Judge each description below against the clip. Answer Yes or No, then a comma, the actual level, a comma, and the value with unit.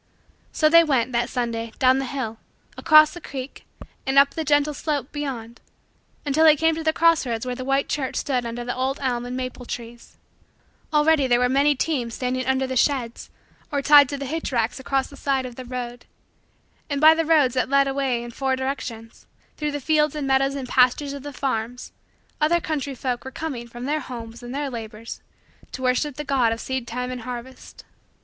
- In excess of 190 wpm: Yes, fast, 205 wpm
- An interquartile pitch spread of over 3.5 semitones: No, average, 2.8 semitones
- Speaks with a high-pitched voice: Yes, very high, 265 Hz